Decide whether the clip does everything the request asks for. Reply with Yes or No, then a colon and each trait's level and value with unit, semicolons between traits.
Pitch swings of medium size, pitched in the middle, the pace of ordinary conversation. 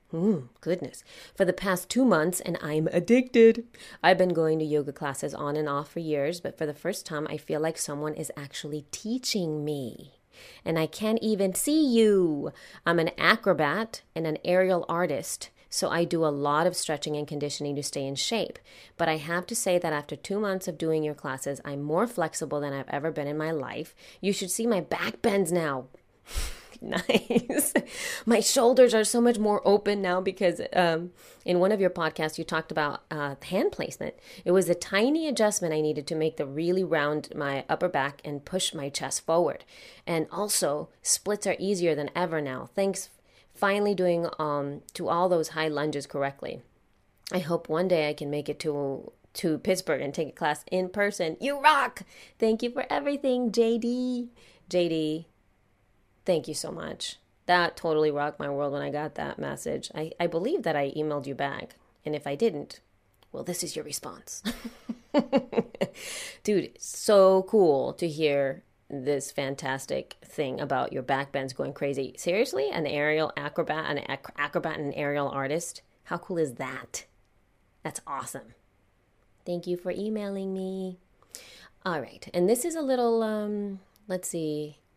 Yes: average, 4.9 semitones; medium, 165 Hz; average, 180 wpm